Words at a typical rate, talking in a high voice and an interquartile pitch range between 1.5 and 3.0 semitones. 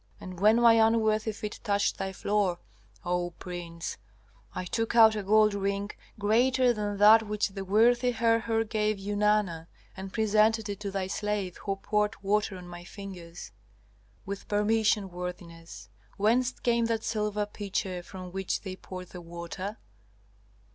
Yes: average, 150 wpm; high, 205 Hz; average, 2.7 semitones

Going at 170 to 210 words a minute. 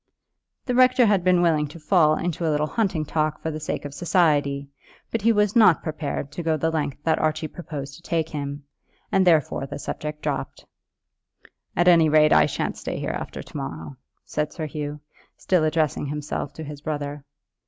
Yes: average, 190 wpm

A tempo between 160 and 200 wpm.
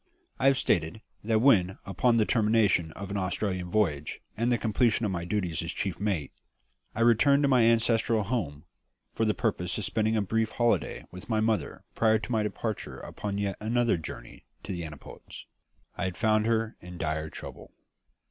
Yes: average, 185 wpm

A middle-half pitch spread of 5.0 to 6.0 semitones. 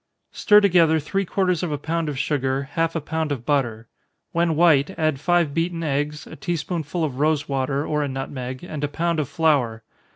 No: average, 3.2 semitones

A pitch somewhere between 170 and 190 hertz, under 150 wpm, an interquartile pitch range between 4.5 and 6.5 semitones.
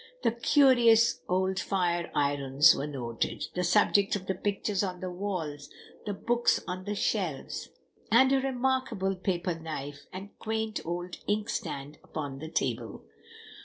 Yes: medium, 185 Hz; average, 140 wpm; average, 5.3 semitones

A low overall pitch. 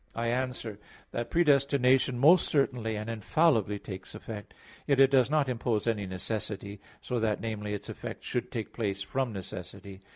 Yes: low, 115 Hz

